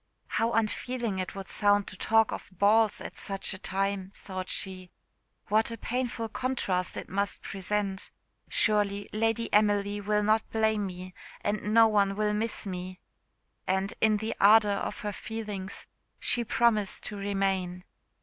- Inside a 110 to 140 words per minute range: No, average, 155 wpm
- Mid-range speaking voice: No, high, 205 Hz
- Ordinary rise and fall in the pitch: No, narrow, 2.2 semitones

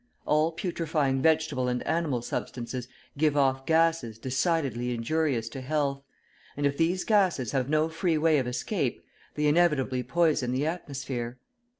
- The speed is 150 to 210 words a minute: No, average, 140 wpm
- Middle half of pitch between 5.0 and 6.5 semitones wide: No, average, 4.0 semitones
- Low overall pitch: No, medium, 145 Hz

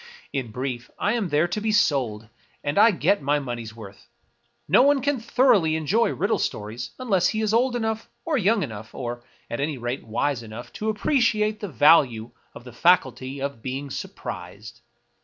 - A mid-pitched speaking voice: Yes, medium, 145 Hz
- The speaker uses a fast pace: No, average, 175 wpm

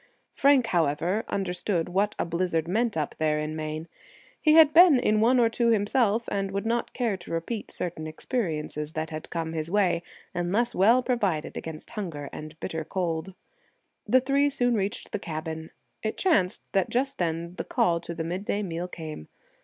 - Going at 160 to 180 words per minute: Yes, average, 175 wpm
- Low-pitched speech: No, medium, 185 Hz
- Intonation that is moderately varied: No, wide, 6.0 semitones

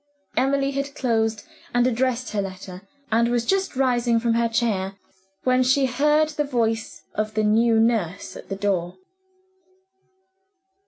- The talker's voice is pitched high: Yes, high, 235 Hz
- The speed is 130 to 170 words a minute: Yes, average, 145 wpm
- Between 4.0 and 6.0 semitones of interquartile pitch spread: No, average, 3.3 semitones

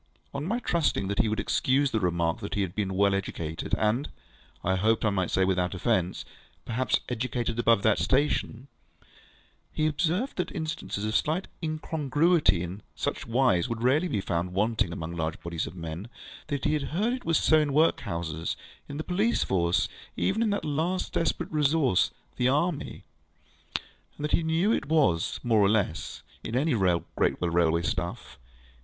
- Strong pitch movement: Yes, wide, 8.9 semitones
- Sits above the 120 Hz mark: No, low, 115 Hz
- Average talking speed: Yes, average, 175 wpm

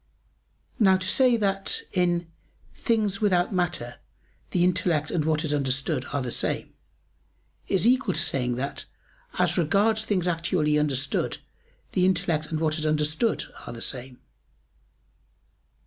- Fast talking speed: No, slow, 135 wpm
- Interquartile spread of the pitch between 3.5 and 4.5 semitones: Yes, average, 4.2 semitones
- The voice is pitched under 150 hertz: No, medium, 170 Hz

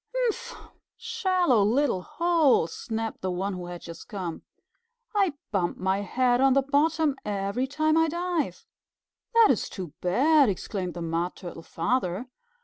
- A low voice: No, high, 245 Hz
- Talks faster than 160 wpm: No, average, 145 wpm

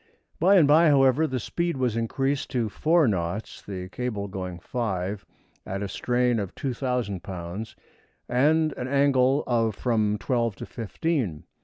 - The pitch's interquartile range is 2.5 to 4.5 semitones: No, average, 5.3 semitones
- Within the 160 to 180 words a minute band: No, average, 150 wpm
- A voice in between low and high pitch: No, low, 120 Hz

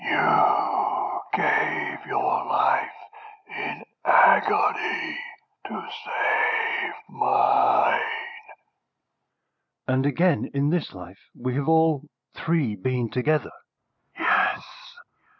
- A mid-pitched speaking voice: Yes, medium, 160 Hz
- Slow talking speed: Yes, slow, 80 wpm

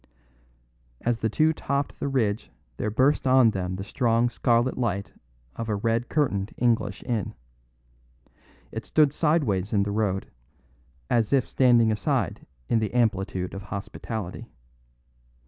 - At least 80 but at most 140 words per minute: Yes, slow, 135 wpm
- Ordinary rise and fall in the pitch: Yes, average, 3.9 semitones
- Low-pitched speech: Yes, low, 115 Hz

